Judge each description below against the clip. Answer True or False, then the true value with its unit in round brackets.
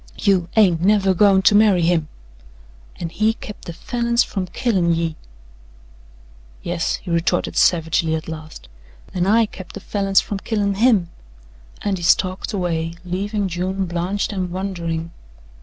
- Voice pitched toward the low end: False (185 Hz)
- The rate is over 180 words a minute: False (145 wpm)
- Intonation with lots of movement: False (3.1 semitones)